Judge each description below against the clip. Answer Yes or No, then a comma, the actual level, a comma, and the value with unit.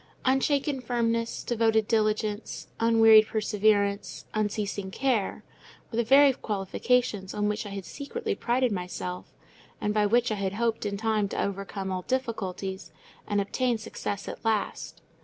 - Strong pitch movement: No, average, 2.8 semitones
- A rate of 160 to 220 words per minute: No, average, 140 wpm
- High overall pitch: Yes, high, 215 Hz